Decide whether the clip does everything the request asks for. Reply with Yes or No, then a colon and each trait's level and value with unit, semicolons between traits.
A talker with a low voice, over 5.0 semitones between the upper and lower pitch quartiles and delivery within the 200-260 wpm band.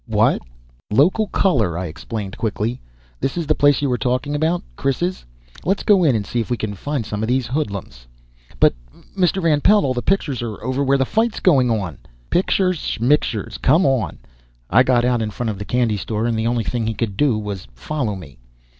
Yes: low, 125 Hz; wide, 5.5 semitones; fast, 205 wpm